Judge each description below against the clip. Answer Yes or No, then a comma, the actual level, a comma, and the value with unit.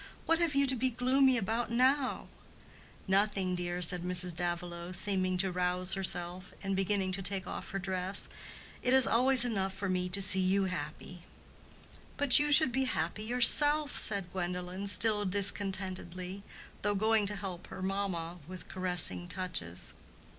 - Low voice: No, high, 190 Hz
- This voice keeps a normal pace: Yes, average, 155 wpm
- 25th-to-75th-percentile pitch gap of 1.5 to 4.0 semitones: Yes, average, 3.5 semitones